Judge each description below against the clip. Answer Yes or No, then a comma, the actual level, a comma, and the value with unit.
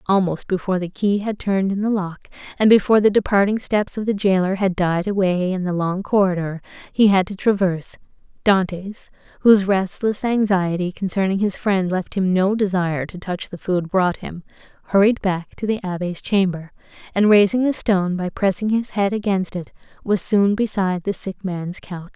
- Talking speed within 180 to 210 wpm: Yes, average, 185 wpm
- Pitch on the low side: No, high, 190 Hz